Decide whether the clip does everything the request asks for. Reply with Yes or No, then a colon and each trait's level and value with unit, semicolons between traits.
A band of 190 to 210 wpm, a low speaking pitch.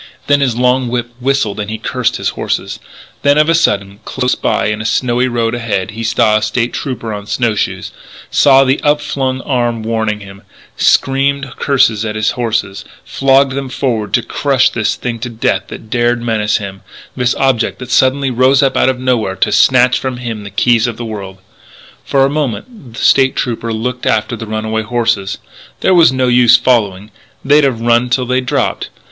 Yes: average, 195 wpm; low, 120 Hz